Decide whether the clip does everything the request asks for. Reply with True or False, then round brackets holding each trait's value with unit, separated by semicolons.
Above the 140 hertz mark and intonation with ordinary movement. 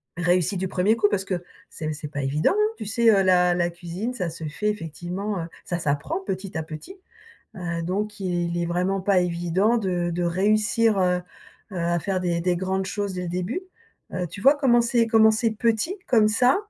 True (185 Hz; 3.6 semitones)